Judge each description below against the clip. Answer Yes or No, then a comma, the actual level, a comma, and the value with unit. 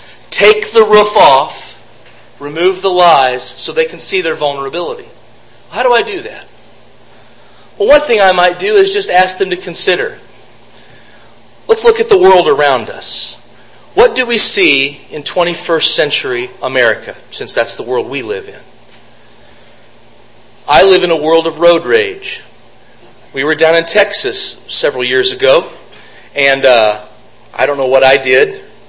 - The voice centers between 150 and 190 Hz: Yes, medium, 185 Hz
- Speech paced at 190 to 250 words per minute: No, average, 160 wpm